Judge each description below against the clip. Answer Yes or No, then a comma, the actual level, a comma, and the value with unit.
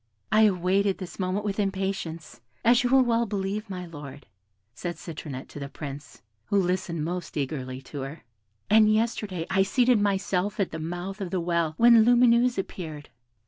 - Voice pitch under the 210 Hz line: Yes, high, 190 Hz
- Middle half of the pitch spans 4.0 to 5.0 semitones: Yes, average, 4.5 semitones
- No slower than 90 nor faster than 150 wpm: No, average, 170 wpm